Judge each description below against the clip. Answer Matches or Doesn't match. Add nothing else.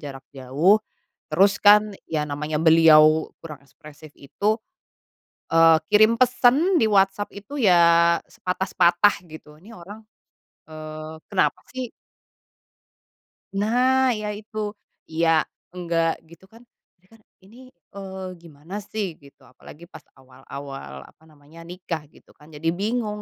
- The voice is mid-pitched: Matches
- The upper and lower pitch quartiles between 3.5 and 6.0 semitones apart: Matches